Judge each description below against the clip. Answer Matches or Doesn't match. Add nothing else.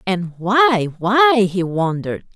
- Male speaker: Doesn't match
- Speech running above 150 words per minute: Doesn't match